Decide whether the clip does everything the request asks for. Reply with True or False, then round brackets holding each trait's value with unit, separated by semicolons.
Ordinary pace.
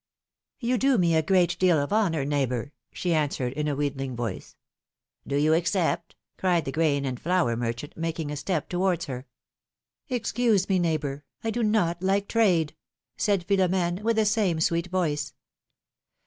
True (170 wpm)